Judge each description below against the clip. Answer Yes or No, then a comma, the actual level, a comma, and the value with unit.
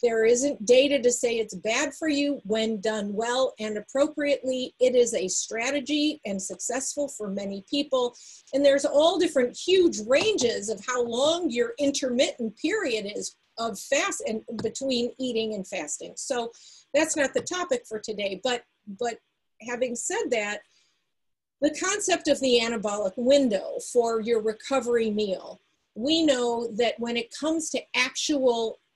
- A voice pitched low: No, very high, 250 Hz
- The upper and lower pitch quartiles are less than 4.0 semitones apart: No, average, 4.3 semitones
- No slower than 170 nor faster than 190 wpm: No, average, 150 wpm